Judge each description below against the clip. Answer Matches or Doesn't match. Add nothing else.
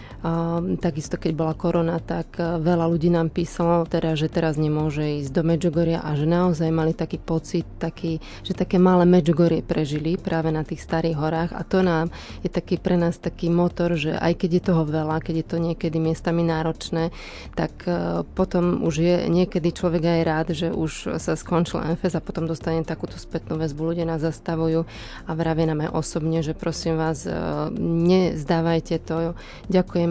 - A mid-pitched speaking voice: Matches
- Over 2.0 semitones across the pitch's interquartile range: Doesn't match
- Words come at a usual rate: Doesn't match